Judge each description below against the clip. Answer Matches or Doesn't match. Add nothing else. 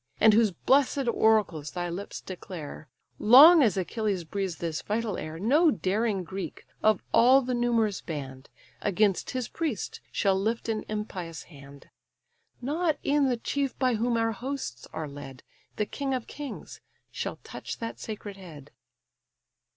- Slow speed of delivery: Doesn't match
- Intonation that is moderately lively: Doesn't match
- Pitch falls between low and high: Doesn't match